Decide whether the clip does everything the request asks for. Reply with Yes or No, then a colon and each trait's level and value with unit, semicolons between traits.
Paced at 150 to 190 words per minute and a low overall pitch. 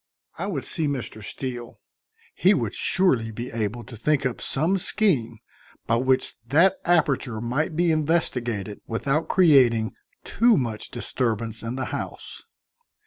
No: average, 140 wpm; low, 130 Hz